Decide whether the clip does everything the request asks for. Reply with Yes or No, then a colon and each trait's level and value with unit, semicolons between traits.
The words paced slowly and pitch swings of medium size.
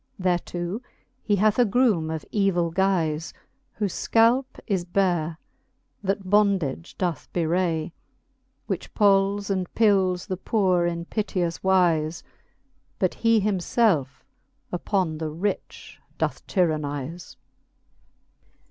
Yes: slow, 110 wpm; average, 3.2 semitones